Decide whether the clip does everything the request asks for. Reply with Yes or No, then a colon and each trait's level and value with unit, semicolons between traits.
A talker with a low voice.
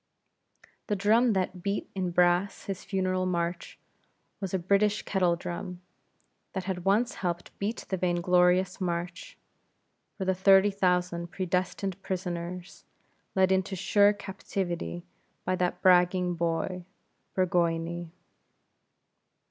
No: medium, 185 Hz